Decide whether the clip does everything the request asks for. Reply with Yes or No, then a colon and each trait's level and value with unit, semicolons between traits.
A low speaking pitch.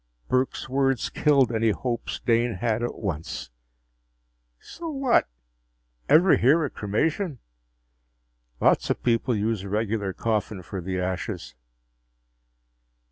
Yes: low, 115 Hz